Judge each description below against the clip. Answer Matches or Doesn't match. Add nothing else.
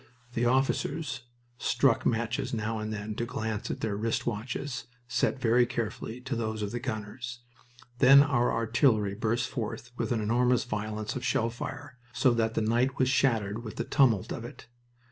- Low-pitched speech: Matches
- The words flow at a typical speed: Matches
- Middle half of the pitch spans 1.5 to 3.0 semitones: Matches